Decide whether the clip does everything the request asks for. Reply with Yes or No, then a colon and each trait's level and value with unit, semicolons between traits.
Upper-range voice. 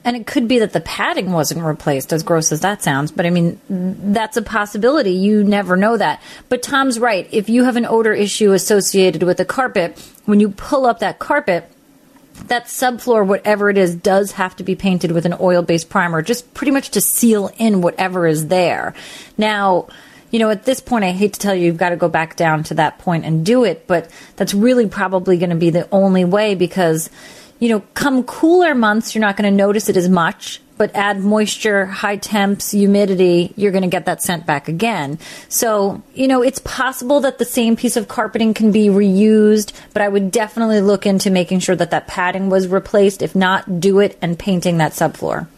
Yes: high, 200 Hz